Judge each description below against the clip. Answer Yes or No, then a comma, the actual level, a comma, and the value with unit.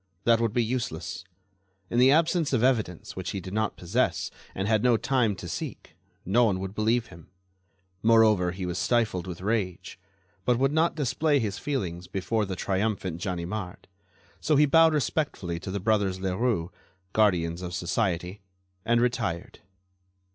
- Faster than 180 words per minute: No, average, 160 wpm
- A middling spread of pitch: Yes, average, 4.8 semitones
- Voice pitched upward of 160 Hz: No, low, 105 Hz